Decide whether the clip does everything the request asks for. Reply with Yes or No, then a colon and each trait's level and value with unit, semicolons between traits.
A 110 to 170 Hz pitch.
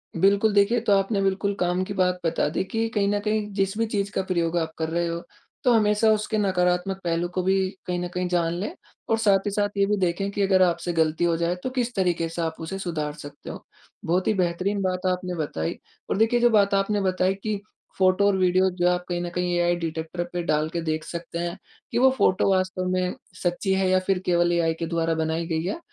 No: medium, 185 Hz